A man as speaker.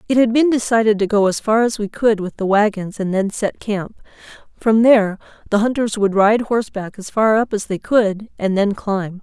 No: female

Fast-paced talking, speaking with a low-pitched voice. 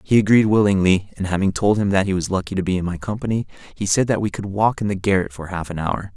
Yes: fast, 280 wpm; very low, 95 Hz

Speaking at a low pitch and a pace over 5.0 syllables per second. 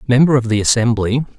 Yes: low, 120 Hz; 6.3 syllables/s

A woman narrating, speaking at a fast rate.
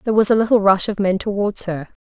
Yes: female; fast, 265 wpm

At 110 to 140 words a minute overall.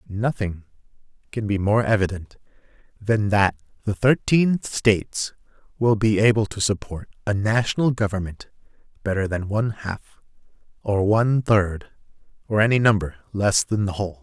Yes: slow, 135 wpm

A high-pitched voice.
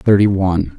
No: very low, 95 Hz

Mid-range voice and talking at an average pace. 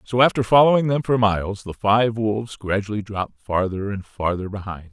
No: low, 105 Hz; average, 185 wpm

